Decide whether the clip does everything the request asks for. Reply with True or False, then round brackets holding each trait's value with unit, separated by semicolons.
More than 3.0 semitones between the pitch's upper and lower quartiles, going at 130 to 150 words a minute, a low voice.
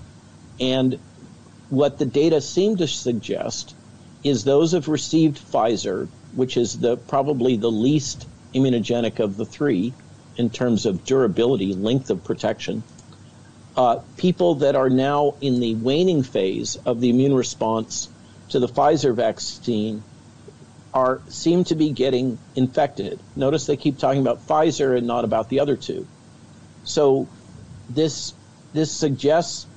True (3.7 semitones; 135 wpm; 130 Hz)